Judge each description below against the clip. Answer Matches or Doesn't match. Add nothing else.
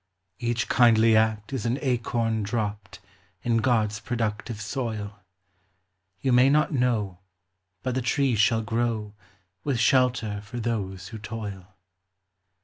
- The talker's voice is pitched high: Doesn't match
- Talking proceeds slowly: Matches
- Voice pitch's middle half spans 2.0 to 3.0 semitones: Matches